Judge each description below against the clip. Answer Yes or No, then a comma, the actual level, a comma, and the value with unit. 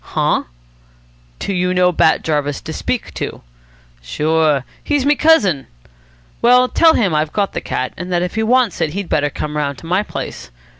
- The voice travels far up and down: Yes, wide, 6.5 semitones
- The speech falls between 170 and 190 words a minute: Yes, average, 185 wpm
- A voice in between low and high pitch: Yes, medium, 180 Hz